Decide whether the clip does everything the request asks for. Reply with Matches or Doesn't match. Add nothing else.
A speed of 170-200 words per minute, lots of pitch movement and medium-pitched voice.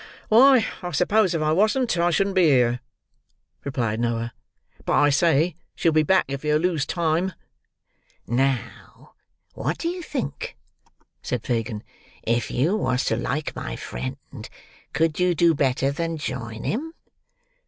Doesn't match